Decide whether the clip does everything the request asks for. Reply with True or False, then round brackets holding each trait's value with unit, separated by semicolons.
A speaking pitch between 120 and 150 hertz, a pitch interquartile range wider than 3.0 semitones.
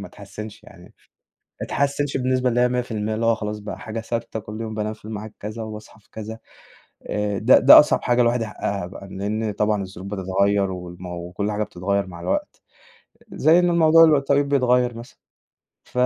False (110 Hz; 3.5 semitones)